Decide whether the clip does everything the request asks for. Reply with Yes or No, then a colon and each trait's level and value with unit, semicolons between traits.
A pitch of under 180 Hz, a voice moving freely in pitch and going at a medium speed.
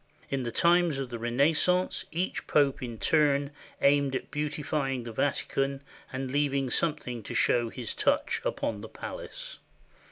No: medium, 140 Hz; average, 3.3 semitones; average, 155 wpm